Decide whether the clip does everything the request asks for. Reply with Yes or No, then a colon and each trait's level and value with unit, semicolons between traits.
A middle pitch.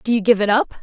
No: high, 215 Hz